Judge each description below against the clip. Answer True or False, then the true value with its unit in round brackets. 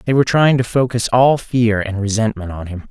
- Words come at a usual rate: False (230 wpm)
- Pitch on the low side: True (115 Hz)